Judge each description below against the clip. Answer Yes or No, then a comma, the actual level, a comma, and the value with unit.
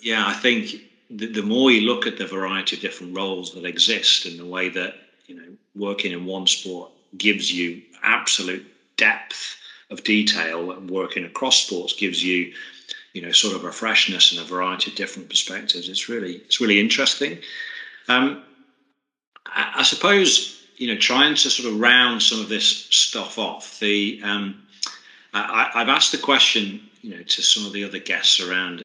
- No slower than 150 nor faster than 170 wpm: No, average, 180 wpm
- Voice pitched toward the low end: Yes, low, 100 Hz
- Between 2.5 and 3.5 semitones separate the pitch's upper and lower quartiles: No, average, 4.8 semitones